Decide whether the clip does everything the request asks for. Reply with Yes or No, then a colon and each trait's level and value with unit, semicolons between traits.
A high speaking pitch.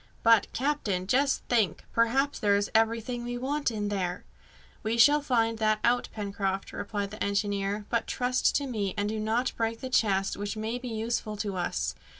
Yes: high, 220 Hz